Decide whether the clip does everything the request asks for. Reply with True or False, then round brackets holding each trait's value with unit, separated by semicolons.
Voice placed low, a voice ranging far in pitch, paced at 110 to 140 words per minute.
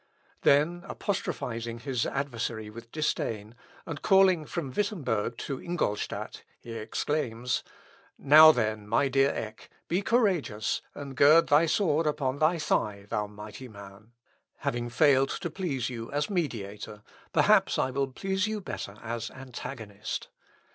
True (130 Hz; 5.7 semitones; 135 wpm)